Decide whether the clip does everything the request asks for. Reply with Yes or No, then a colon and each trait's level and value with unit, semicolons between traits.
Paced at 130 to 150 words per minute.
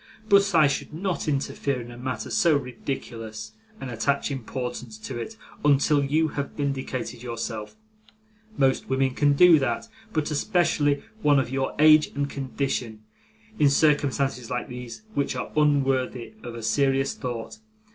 Yes: average, 145 wpm